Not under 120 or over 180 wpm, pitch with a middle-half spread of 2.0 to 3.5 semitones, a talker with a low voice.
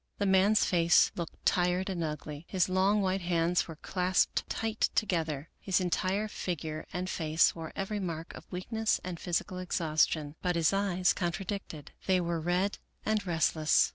No: average, 165 wpm; narrow, 2.6 semitones; medium, 180 Hz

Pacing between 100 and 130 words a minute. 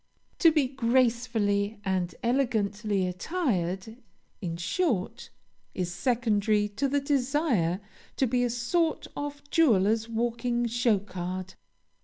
Yes: slow, 110 wpm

